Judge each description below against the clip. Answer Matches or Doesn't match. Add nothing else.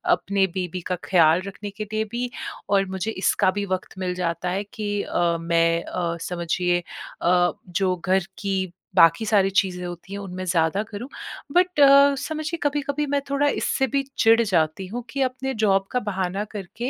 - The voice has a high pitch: Matches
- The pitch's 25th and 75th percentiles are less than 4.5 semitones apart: Doesn't match